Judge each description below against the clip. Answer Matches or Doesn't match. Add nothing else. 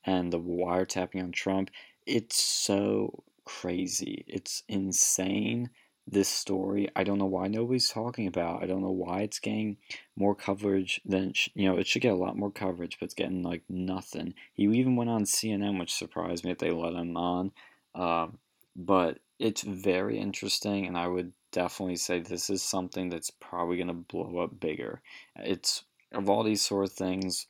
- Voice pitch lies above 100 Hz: Doesn't match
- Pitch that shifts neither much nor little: Doesn't match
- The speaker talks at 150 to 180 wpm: Matches